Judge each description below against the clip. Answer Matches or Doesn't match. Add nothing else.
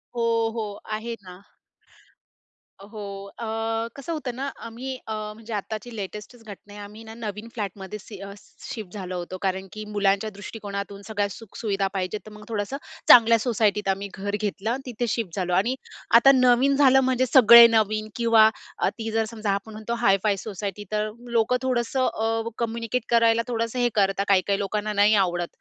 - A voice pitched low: Doesn't match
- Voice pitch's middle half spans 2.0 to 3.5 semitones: Matches